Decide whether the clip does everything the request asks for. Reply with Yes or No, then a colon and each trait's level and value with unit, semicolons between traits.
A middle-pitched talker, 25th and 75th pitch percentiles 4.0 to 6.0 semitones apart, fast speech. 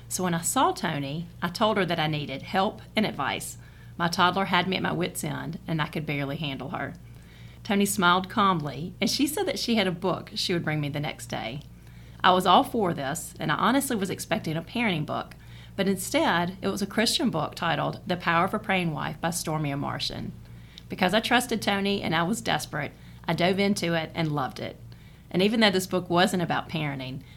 Yes: medium, 175 Hz; average, 4.9 semitones; fast, 215 wpm